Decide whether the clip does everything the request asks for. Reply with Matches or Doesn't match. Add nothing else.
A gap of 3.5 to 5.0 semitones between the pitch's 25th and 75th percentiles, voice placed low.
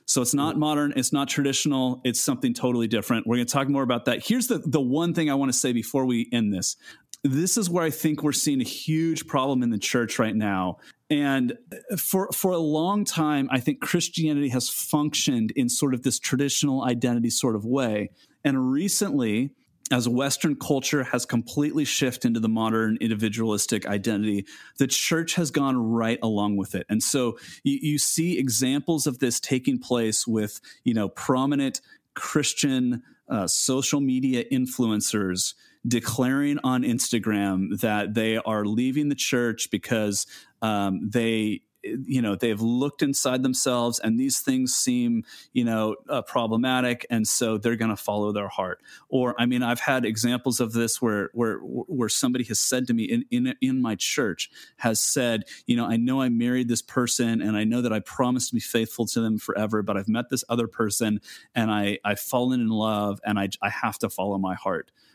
Matches